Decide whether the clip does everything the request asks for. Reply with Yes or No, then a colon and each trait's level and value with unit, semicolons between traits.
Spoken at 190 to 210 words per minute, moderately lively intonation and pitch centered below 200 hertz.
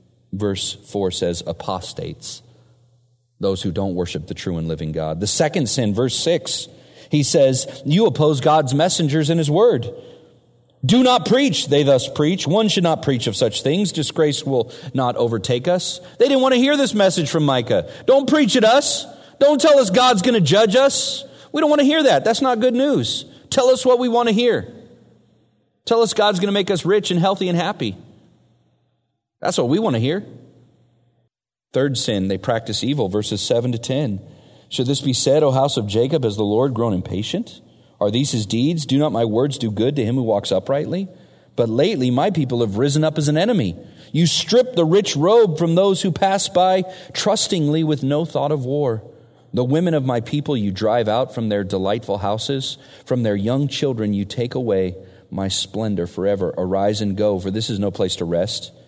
No: average, 200 wpm; wide, 8.8 semitones; medium, 140 Hz